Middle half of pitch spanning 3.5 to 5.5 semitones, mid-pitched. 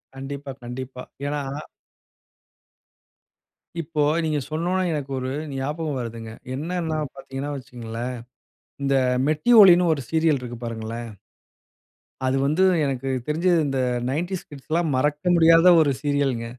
Yes: average, 3.8 semitones; medium, 145 Hz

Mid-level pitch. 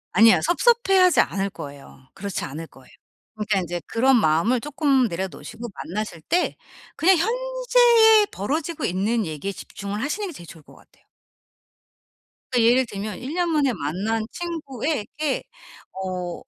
No: high, 230 Hz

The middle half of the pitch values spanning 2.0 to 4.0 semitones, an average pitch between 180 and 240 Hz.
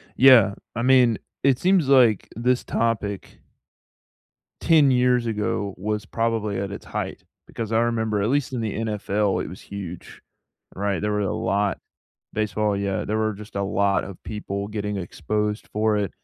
No: narrow, 2.6 semitones; low, 105 Hz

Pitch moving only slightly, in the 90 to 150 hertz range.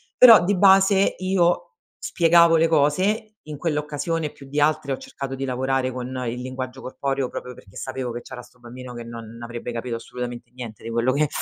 No: average, 5.1 semitones; low, 135 Hz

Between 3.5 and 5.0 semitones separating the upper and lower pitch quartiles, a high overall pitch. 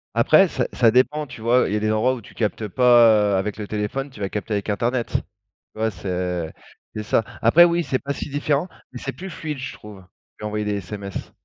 No: average, 4.0 semitones; low, 110 Hz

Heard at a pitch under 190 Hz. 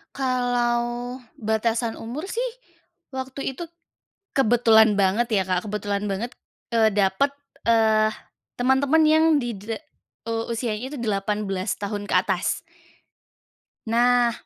No: high, 230 Hz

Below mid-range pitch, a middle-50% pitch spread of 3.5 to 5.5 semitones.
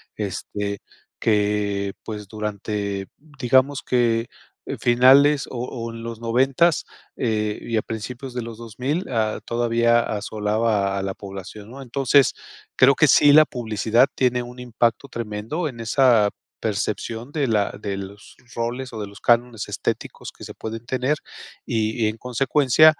No: low, 115 Hz; average, 3.1 semitones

